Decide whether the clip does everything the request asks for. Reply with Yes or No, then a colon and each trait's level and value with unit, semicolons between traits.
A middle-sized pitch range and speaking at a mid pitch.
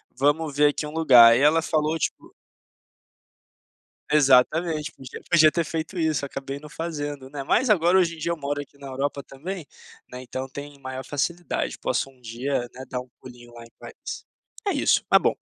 Yes: average, 3.4 semitones; medium, 145 Hz